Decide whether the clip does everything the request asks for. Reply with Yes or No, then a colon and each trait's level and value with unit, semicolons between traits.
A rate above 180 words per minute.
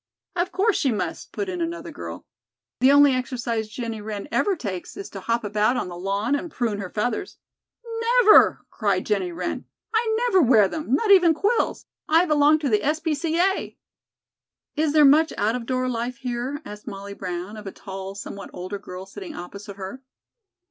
Yes: average, 190 wpm